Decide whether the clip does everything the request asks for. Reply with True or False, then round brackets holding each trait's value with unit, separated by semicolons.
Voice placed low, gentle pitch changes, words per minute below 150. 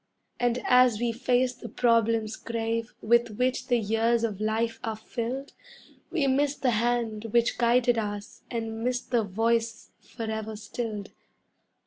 False (230 Hz; 1.7 semitones; 140 wpm)